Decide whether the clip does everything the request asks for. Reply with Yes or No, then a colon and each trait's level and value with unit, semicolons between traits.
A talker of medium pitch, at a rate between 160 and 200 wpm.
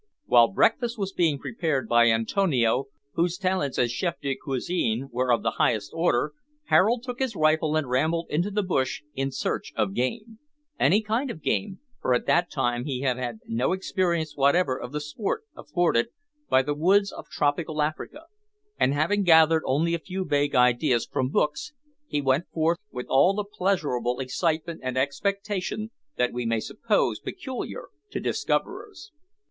Yes: medium, 155 Hz; average, 165 wpm